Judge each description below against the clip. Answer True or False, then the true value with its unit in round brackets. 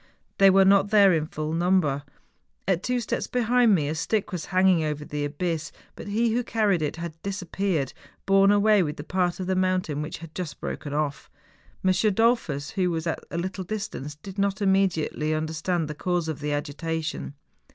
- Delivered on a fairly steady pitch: False (4.2 semitones)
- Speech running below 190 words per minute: False (205 wpm)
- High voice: False (180 Hz)